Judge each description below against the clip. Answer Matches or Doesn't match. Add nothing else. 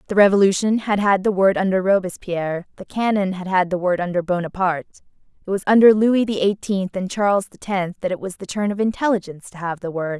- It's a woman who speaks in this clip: Matches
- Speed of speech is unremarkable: Doesn't match